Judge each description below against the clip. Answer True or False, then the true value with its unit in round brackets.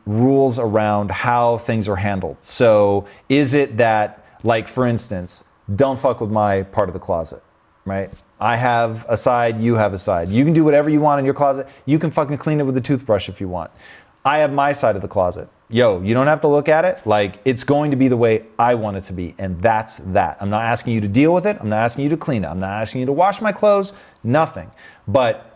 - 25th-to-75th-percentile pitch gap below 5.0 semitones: False (5.4 semitones)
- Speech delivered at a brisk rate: True (245 wpm)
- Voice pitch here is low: True (115 Hz)